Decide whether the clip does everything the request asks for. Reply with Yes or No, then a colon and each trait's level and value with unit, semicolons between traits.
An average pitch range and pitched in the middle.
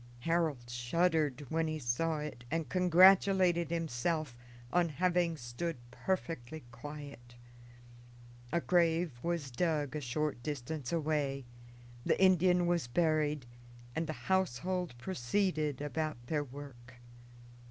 Yes: average, 3.9 semitones; medium, 155 Hz